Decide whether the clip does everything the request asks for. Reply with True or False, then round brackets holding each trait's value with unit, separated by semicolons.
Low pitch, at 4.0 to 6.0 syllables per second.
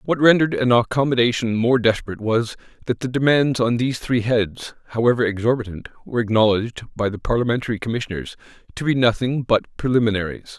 False (120 Hz; 6.4 syllables/s)